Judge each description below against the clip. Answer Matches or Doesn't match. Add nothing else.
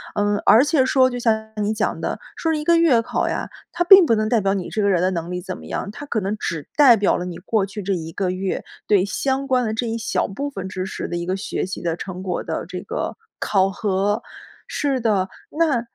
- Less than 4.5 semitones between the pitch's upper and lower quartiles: Doesn't match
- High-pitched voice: Matches